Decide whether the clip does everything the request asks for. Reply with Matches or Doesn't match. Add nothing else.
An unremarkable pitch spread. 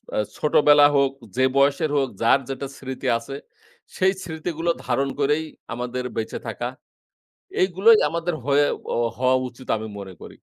Matches